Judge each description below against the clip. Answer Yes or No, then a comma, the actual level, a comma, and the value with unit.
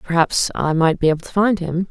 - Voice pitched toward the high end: No, medium, 175 Hz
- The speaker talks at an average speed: No, fast, 250 wpm